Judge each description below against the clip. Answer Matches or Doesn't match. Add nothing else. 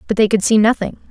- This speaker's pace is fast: Matches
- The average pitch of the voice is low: Doesn't match